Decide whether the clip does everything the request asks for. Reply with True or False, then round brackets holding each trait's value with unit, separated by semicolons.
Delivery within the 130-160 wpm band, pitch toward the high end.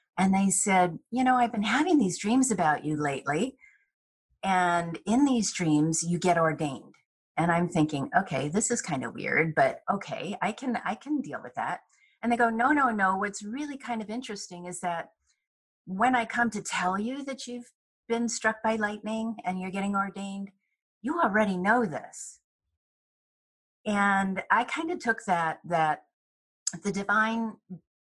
False (170 wpm; 200 Hz)